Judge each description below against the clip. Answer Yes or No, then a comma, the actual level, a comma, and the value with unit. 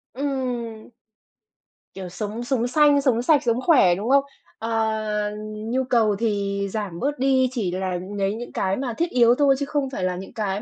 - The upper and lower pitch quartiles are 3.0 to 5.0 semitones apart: Yes, average, 4.4 semitones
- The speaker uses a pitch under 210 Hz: No, high, 230 Hz